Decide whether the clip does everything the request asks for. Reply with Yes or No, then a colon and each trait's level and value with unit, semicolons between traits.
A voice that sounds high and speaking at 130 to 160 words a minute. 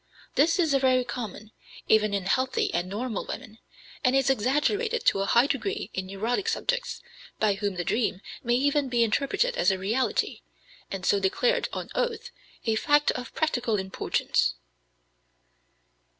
Yes: high, 245 Hz; average, 150 wpm